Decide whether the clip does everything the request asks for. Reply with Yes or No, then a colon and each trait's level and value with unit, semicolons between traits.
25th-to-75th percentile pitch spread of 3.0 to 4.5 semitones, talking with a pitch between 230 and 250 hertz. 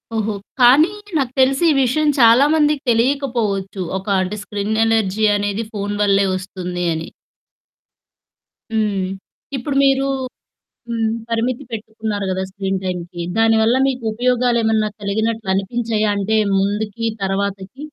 No: average, 3.4 semitones; high, 220 Hz